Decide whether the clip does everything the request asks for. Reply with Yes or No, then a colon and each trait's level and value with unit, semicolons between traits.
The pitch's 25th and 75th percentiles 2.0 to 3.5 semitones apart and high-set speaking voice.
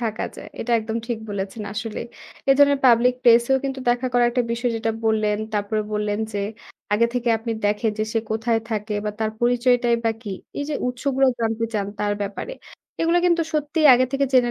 Yes: average, 2.9 semitones; high, 235 Hz